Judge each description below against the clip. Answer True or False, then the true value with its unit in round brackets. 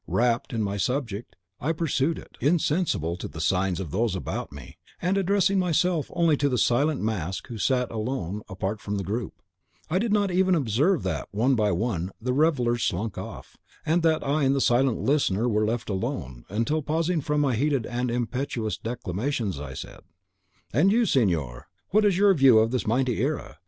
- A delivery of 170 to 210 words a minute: True (190 wpm)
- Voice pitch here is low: True (125 Hz)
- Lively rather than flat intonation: True (6.6 semitones)